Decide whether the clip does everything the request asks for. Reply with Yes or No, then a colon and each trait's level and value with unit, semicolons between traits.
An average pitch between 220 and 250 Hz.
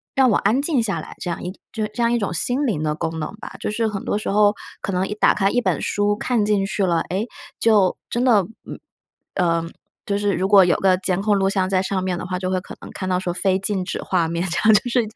No: high, 195 Hz